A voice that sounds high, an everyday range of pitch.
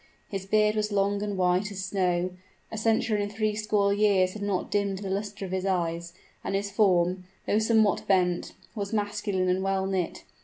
No: high, 200 Hz; narrow, 2.0 semitones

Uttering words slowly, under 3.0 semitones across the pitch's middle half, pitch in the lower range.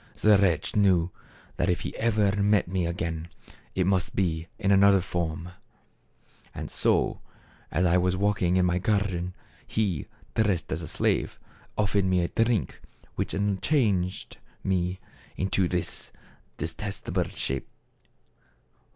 Yes: slow, 125 wpm; narrow, 2.4 semitones; very low, 95 Hz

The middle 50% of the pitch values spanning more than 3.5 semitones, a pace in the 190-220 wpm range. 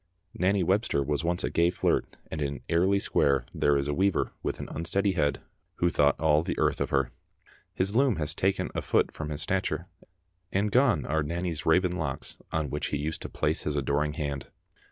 Yes: average, 4.2 semitones; average, 200 wpm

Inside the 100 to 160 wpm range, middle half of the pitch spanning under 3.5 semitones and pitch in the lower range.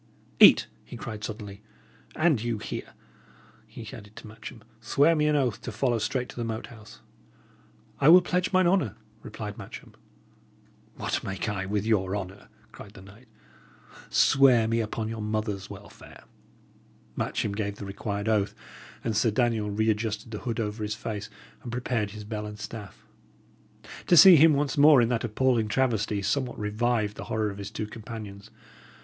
No: average, 170 wpm; average, 2.7 semitones; low, 110 Hz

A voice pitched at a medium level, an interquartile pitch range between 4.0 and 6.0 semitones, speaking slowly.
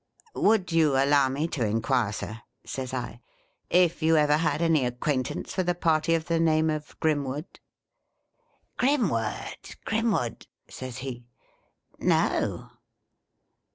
No: medium, 150 Hz; average, 4.3 semitones; average, 155 wpm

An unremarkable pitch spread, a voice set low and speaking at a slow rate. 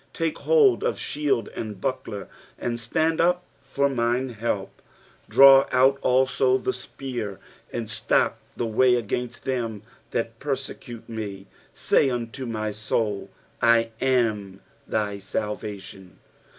Yes: average, 3.6 semitones; low, 120 Hz; slow, 130 wpm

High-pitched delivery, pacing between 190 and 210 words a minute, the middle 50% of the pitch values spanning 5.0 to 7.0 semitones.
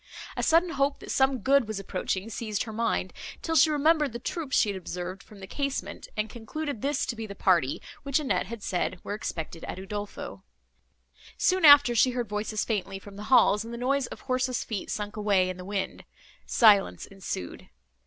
Yes: high, 220 Hz; average, 195 wpm; wide, 5.5 semitones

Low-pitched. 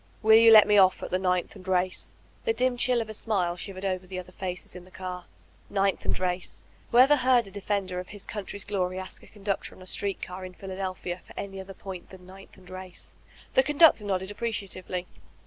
No: high, 190 Hz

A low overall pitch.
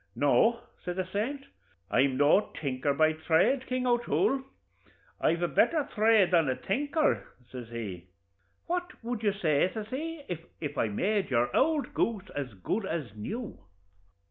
No: high, 190 Hz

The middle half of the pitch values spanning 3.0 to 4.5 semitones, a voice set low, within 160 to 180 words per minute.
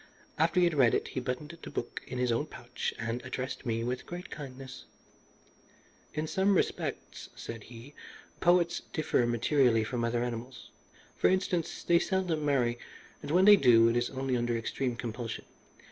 No: average, 5.1 semitones; low, 130 Hz; average, 170 wpm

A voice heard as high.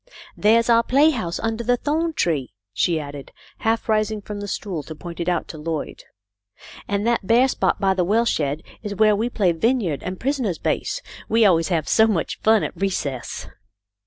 Yes: high, 205 Hz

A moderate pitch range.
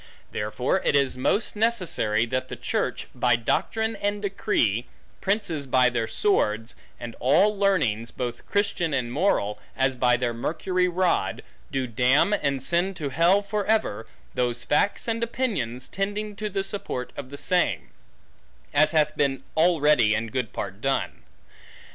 No: wide, 8.2 semitones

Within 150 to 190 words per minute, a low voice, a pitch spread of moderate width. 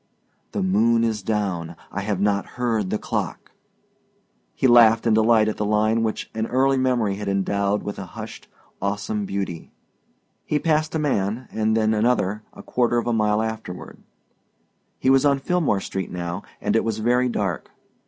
Yes: average, 170 wpm; low, 110 Hz; average, 3.0 semitones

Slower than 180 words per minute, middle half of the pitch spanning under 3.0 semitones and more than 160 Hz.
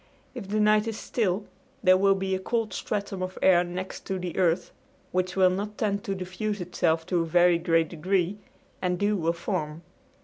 No: average, 195 wpm; narrow, 2.4 semitones; medium, 185 Hz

